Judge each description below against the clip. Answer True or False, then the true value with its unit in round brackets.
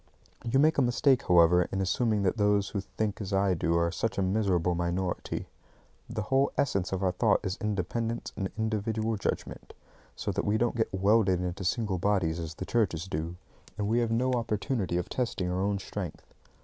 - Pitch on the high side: False (100 Hz)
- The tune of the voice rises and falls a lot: False (3.8 semitones)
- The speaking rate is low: False (190 wpm)